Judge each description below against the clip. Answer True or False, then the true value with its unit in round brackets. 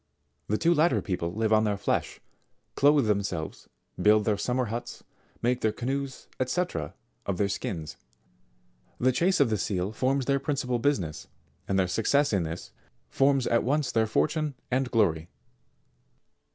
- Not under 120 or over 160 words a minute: True (155 wpm)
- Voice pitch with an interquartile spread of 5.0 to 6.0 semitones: True (5.4 semitones)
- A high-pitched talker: False (115 Hz)